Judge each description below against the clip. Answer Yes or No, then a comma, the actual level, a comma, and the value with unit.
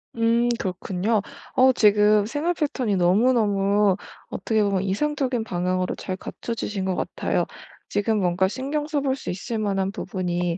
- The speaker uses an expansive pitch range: No, average, 4.2 semitones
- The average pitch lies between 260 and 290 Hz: No, high, 210 Hz